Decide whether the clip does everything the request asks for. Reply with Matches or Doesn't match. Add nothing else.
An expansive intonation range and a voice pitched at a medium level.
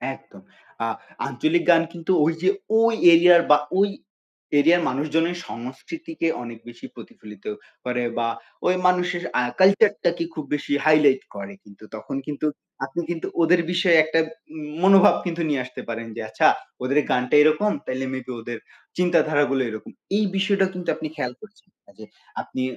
Matches